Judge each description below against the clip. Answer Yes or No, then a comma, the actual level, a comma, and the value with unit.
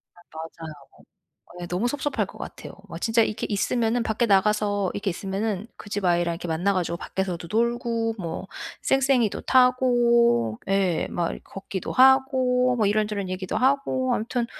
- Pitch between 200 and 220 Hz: Yes, high, 215 Hz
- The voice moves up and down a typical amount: Yes, average, 4.6 semitones